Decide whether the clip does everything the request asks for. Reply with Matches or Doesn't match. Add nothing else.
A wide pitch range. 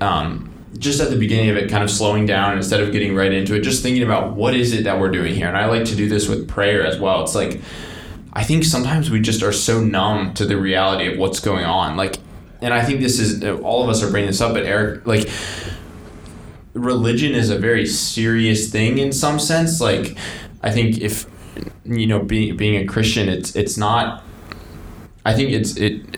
Doesn't match